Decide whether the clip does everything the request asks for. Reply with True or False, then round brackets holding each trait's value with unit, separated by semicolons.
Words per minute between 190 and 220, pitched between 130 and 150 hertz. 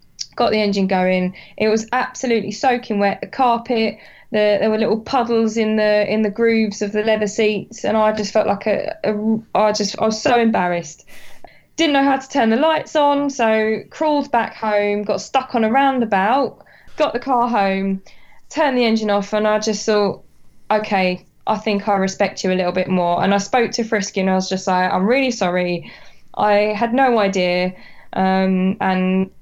False (195 wpm; 215 Hz)